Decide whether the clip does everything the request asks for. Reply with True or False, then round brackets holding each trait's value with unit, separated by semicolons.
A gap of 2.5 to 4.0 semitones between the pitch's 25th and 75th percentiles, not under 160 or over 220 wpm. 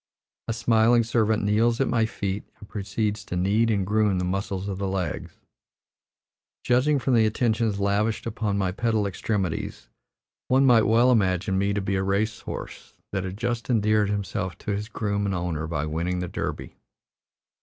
True (2.8 semitones; 175 wpm)